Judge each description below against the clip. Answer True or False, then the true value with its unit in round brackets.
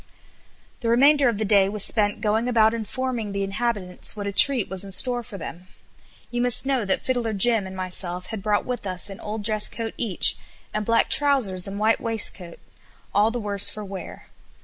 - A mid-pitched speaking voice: False (215 Hz)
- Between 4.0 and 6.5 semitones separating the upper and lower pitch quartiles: False (3.2 semitones)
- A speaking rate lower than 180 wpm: False (200 wpm)